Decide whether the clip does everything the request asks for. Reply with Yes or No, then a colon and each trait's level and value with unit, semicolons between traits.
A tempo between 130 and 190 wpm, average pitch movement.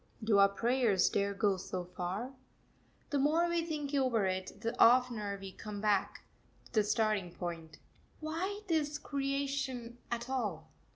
No: average, 150 wpm; wide, 5.7 semitones